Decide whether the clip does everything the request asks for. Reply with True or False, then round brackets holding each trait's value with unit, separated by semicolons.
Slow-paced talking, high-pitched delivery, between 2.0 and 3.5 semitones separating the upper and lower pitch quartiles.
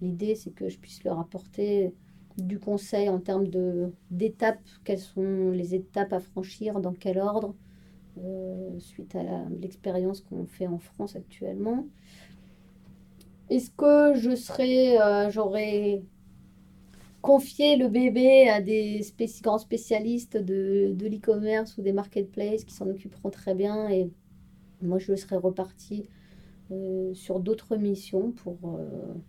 True (135 wpm; 195 Hz; 2.5 semitones)